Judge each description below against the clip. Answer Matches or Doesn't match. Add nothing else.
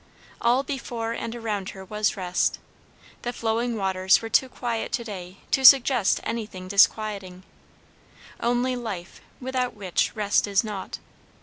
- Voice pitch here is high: Matches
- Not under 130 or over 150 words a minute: Matches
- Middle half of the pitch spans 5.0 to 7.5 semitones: Doesn't match